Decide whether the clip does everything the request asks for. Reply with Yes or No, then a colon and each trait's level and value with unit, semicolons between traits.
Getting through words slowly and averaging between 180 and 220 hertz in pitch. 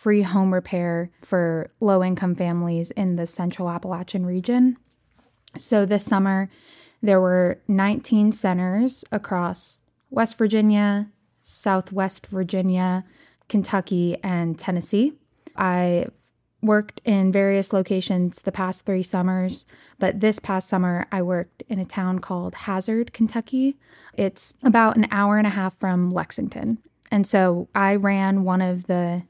Yes: slow, 130 wpm; high, 190 Hz